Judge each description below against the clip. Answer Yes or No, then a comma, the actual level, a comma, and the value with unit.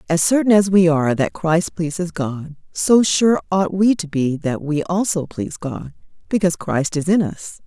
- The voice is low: No, medium, 170 Hz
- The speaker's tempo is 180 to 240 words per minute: Yes, average, 195 wpm